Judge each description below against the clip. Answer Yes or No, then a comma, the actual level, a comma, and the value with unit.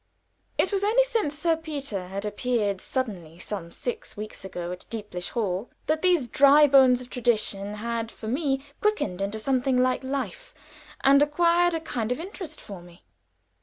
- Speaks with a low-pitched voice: No, very high, 250 Hz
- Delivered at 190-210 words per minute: No, average, 170 wpm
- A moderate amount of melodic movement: No, wide, 6.6 semitones